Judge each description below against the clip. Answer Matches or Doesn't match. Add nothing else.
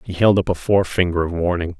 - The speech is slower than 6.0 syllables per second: Doesn't match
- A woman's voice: Doesn't match